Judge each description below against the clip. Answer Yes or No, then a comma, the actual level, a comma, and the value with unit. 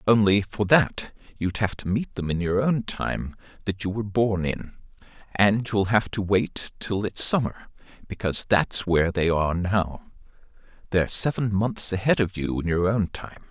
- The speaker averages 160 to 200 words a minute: Yes, average, 180 wpm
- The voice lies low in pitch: Yes, low, 100 Hz